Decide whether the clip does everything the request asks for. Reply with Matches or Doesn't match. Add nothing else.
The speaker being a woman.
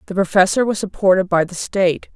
Matches